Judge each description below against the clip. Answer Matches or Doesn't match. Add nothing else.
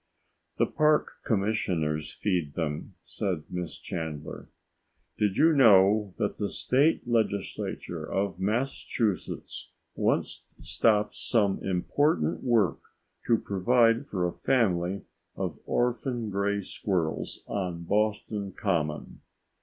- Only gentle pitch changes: Doesn't match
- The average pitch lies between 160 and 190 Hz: Doesn't match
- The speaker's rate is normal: Doesn't match